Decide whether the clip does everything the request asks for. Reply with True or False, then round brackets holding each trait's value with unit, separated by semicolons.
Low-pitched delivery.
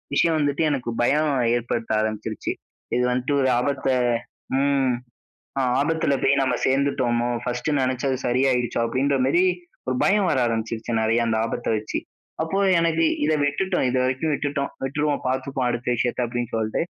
True (130 Hz)